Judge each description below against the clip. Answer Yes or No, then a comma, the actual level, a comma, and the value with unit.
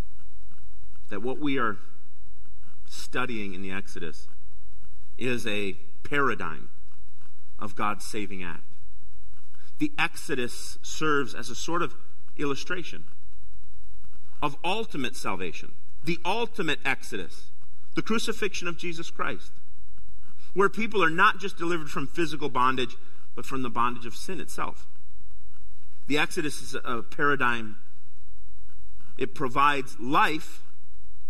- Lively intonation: Yes, wide, 6.7 semitones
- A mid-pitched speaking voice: No, very low, 95 Hz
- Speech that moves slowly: Yes, slow, 110 wpm